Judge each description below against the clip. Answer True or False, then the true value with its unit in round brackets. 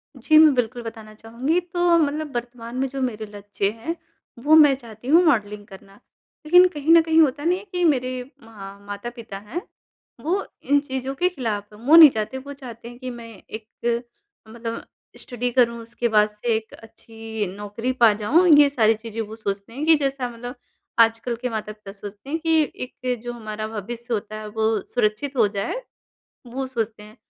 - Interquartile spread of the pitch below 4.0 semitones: False (4.4 semitones)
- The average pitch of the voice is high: True (235 Hz)